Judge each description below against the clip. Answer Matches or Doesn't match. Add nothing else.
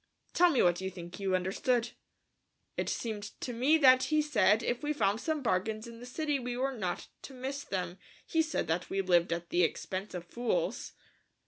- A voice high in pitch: Matches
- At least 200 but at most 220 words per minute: Matches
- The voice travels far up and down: Matches